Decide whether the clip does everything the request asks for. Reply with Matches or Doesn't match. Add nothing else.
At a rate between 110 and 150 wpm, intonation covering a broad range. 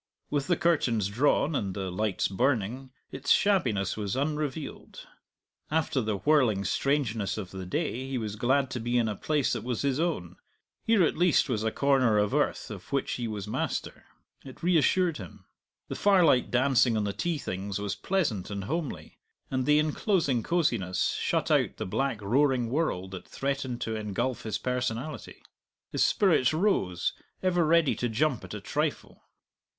Doesn't match